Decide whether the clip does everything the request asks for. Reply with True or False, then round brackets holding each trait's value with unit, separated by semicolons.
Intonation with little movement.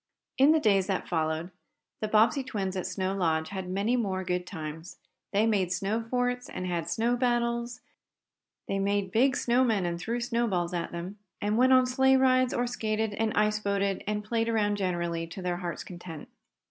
False (4.7 semitones)